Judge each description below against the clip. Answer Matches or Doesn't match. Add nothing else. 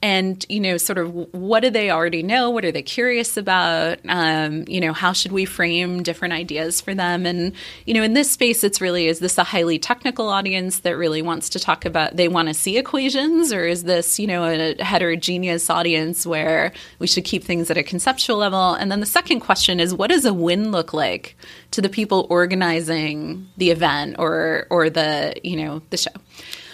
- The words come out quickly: Matches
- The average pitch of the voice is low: Doesn't match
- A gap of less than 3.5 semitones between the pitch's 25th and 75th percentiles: Matches